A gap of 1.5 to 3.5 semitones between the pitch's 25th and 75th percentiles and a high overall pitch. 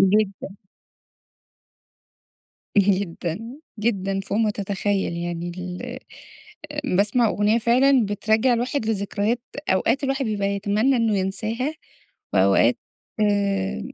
Yes: average, 3.1 semitones; high, 205 Hz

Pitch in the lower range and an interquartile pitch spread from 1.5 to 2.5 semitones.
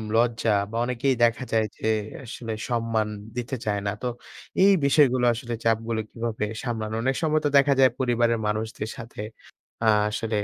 Yes: low, 115 Hz; narrow, 2.1 semitones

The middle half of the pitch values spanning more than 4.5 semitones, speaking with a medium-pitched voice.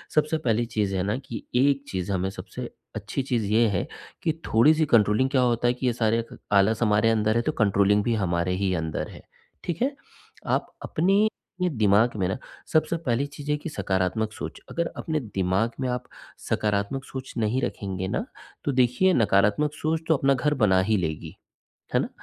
No: wide, 5.5 semitones; low, 115 Hz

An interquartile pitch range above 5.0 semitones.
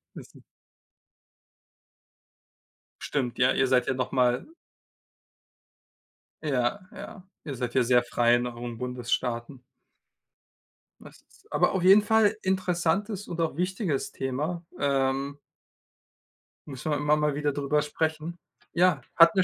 Yes: wide, 5.4 semitones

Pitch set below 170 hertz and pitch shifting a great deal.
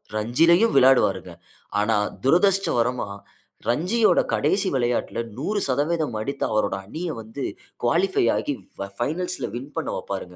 Yes: medium, 140 Hz; wide, 6.9 semitones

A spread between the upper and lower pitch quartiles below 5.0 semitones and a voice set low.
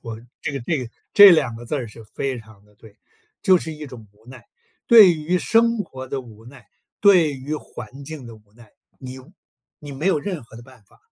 No: wide, 5.5 semitones; low, 130 Hz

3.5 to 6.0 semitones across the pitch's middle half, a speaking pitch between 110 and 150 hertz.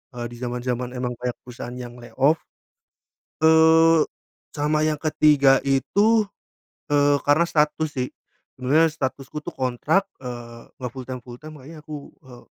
Yes: average, 3.8 semitones; medium, 140 Hz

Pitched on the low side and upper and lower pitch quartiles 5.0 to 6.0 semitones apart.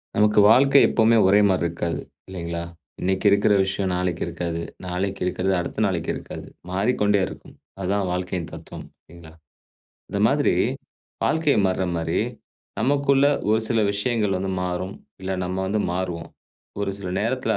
No: very low, 95 Hz; average, 2.9 semitones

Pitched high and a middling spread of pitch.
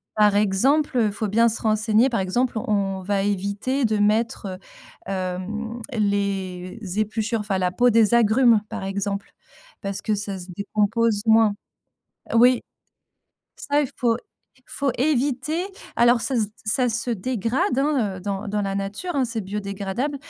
Yes: high, 215 Hz; average, 3.3 semitones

